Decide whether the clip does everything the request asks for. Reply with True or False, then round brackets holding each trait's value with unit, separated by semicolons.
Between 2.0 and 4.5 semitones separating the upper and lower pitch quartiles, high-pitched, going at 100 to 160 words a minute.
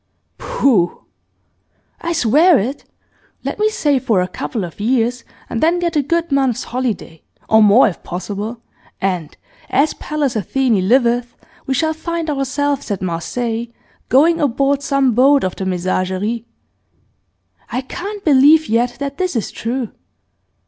False (4.9 semitones; 255 Hz; 140 wpm)